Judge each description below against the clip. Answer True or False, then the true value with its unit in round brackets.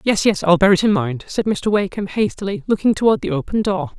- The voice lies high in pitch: True (215 Hz)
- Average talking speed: False (240 wpm)